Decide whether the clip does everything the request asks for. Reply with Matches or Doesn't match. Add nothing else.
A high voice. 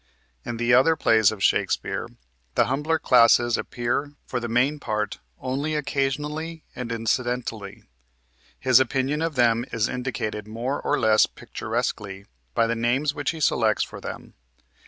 Doesn't match